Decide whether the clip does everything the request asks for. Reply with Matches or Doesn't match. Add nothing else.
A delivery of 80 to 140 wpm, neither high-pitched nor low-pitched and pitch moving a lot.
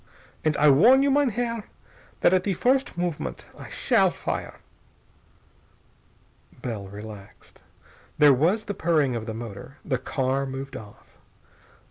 Matches